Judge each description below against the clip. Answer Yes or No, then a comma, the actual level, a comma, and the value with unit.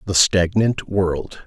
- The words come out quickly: No, slow, 125 wpm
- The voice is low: Yes, very low, 95 Hz